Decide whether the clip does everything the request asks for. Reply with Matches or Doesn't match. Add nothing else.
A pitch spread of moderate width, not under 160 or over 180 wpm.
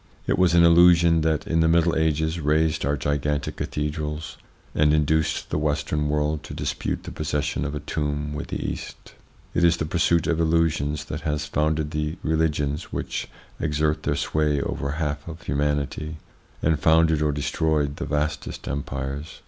Doesn't match